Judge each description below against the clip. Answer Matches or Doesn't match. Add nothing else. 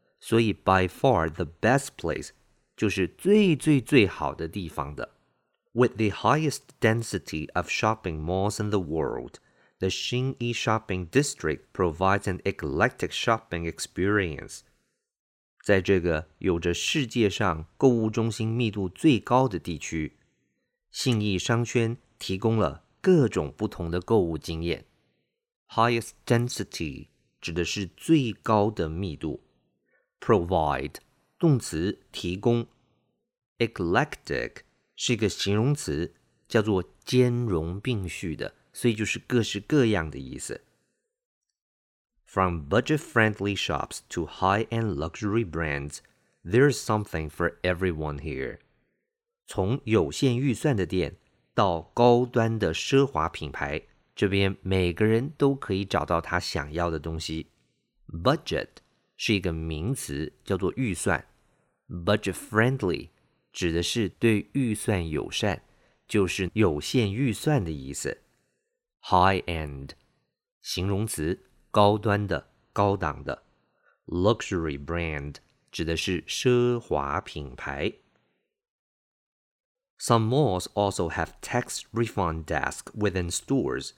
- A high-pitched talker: Doesn't match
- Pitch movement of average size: Doesn't match